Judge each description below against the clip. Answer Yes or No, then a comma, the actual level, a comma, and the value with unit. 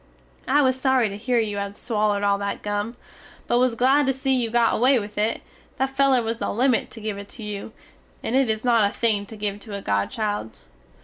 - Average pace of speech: No, fast, 225 wpm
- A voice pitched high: Yes, high, 225 Hz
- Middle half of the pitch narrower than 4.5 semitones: Yes, average, 3.7 semitones